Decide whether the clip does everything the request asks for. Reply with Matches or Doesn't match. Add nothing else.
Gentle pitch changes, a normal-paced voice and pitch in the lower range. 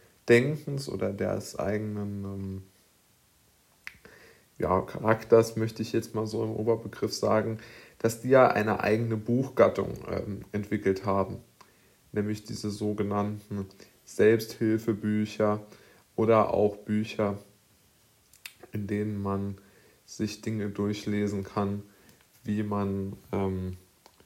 Doesn't match